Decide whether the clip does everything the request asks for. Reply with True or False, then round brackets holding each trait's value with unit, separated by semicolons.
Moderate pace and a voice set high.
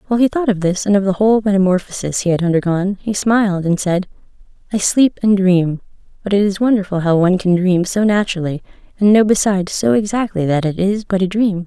False (215 wpm; 195 Hz)